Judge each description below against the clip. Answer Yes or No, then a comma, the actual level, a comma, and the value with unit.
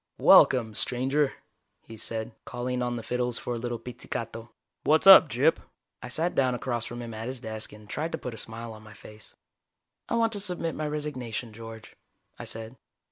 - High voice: No, low, 120 Hz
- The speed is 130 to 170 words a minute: No, average, 190 wpm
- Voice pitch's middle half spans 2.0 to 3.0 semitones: No, average, 3.4 semitones